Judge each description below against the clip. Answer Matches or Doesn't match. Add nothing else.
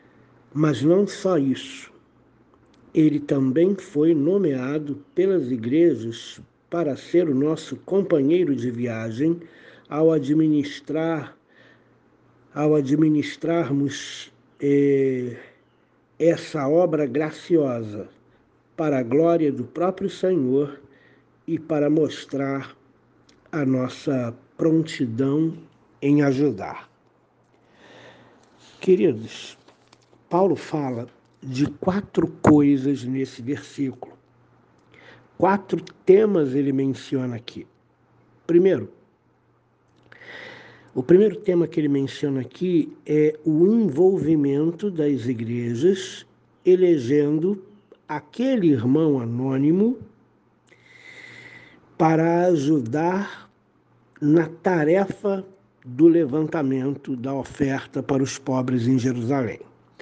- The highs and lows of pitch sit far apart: Doesn't match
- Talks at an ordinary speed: Doesn't match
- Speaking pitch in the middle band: Matches